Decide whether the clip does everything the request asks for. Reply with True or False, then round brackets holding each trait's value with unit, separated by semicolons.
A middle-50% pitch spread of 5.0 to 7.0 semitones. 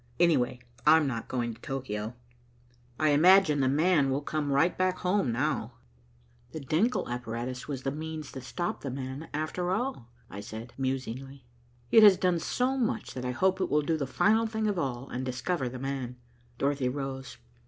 True (5.4 semitones)